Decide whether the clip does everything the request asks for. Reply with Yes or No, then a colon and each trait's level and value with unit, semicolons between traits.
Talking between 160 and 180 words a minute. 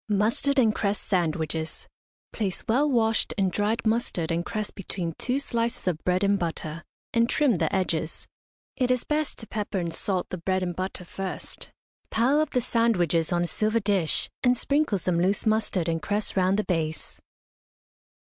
Yes: average, 175 wpm